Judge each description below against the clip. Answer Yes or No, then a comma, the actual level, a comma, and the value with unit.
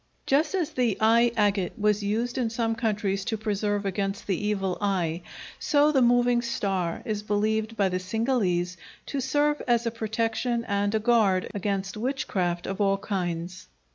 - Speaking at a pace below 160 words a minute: No, average, 165 wpm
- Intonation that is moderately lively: Yes, average, 3.3 semitones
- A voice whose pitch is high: Yes, high, 210 Hz